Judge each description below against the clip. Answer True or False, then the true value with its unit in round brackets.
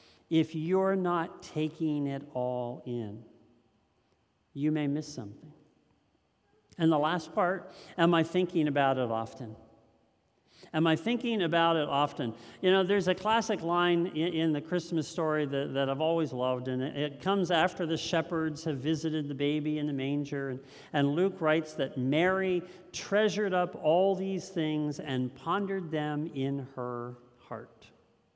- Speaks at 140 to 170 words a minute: True (155 wpm)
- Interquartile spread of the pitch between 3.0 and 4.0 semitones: False (4.4 semitones)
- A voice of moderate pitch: True (155 Hz)